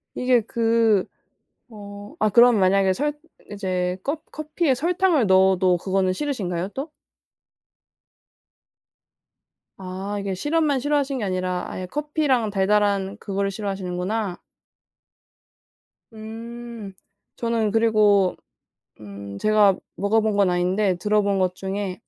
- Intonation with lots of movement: No, average, 3.7 semitones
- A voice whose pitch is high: Yes, high, 205 Hz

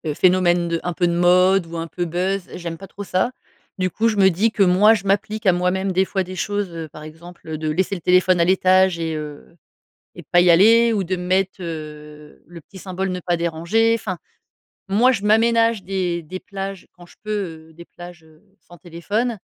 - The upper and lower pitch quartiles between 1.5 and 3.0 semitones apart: Yes, narrow, 2.5 semitones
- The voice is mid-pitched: Yes, medium, 180 Hz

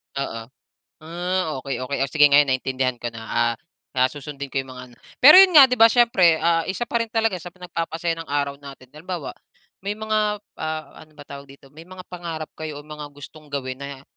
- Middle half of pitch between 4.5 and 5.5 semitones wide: Yes, average, 4.8 semitones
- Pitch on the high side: No, medium, 155 Hz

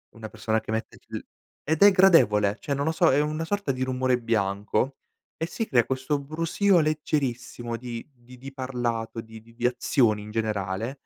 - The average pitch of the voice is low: Yes, low, 125 Hz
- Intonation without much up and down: No, average, 4.8 semitones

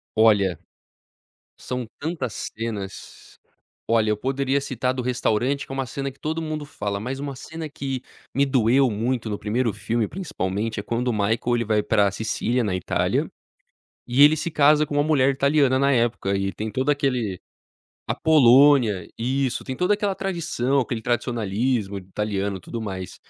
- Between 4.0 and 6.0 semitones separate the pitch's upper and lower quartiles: Yes, average, 4.5 semitones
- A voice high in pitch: No, low, 125 Hz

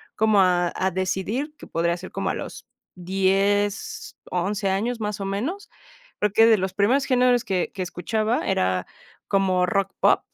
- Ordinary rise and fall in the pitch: Yes, average, 3.1 semitones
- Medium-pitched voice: No, high, 195 Hz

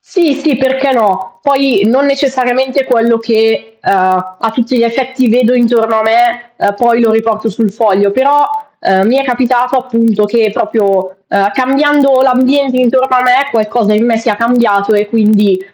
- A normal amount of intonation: Yes, average, 3.0 semitones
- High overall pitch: Yes, high, 235 Hz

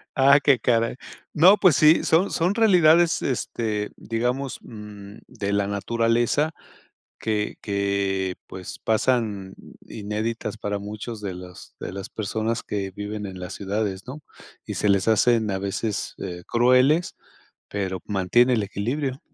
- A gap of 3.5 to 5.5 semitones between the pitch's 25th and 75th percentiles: Yes, average, 4.2 semitones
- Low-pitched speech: Yes, low, 110 Hz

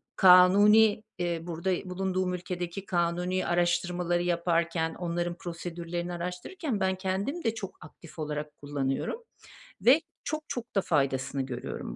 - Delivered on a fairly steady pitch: Yes, narrow, 2.1 semitones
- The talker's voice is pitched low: No, medium, 175 Hz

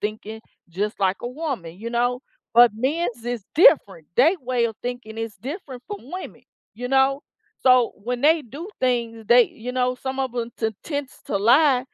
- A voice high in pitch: Yes, high, 245 Hz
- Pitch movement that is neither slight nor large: Yes, average, 3.0 semitones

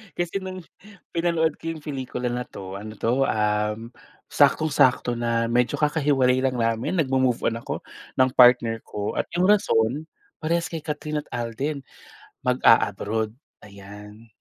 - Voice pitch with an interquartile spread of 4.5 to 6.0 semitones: Yes, average, 4.9 semitones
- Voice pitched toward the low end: Yes, low, 125 Hz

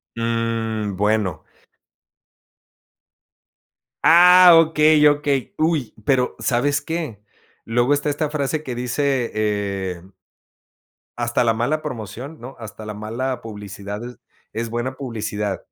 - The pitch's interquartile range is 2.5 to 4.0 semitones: No, average, 5.1 semitones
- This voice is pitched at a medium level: No, low, 120 Hz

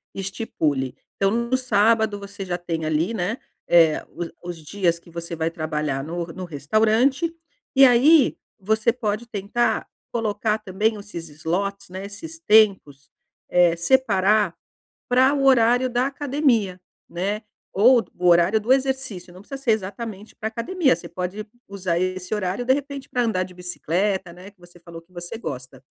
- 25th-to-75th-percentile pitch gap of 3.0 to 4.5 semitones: No, average, 5.0 semitones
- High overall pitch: Yes, high, 200 Hz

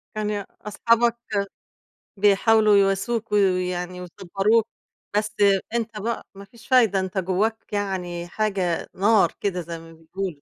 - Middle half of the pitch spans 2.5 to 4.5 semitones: Yes, average, 3.0 semitones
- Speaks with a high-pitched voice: Yes, high, 200 Hz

